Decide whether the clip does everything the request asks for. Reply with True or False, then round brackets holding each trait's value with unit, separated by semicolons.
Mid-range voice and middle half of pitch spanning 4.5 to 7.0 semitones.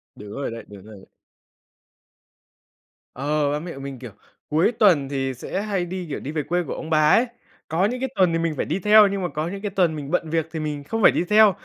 True (160 Hz; 5.3 semitones)